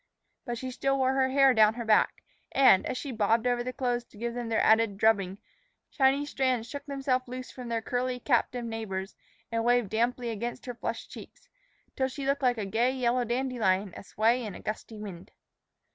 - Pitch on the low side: No, high, 240 Hz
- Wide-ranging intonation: No, narrow, 2.6 semitones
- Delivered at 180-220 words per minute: Yes, average, 200 wpm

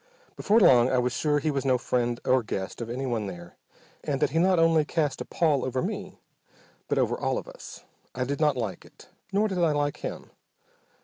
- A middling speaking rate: No, fast, 210 wpm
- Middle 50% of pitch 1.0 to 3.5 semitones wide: No, average, 5.0 semitones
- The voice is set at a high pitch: No, medium, 140 Hz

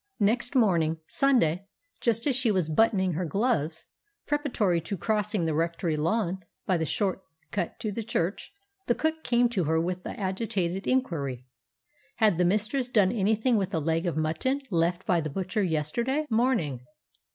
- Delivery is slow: No, average, 165 wpm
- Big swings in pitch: Yes, wide, 5.7 semitones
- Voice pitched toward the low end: No, high, 190 Hz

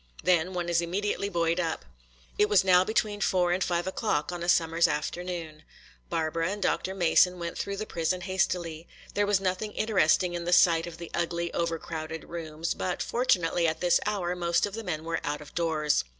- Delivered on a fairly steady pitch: Yes, narrow, 2.2 semitones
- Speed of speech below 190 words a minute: No, average, 195 wpm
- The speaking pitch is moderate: Yes, medium, 175 Hz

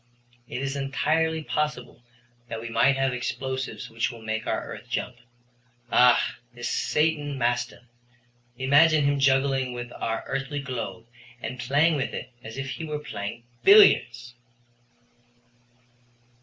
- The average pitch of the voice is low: Yes, low, 130 Hz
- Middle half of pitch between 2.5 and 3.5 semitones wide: Yes, average, 3.0 semitones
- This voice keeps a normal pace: No, slow, 130 wpm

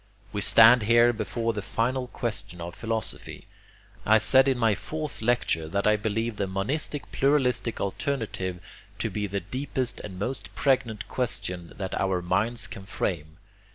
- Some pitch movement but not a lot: Yes, average, 4.1 semitones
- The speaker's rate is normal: Yes, average, 155 wpm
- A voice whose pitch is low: Yes, low, 110 Hz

